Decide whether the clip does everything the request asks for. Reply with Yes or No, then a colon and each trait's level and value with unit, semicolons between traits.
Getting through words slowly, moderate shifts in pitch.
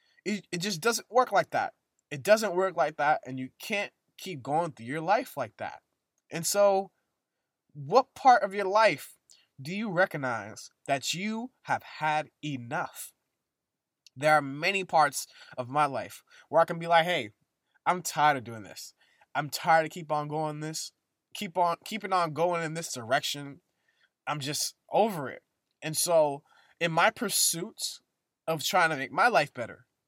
No: average, 170 wpm; average, 4.7 semitones